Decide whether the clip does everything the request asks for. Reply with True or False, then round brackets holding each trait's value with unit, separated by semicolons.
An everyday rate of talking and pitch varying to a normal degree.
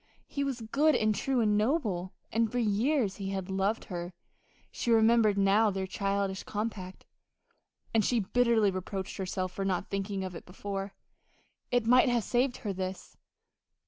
True (160 wpm; 3.4 semitones)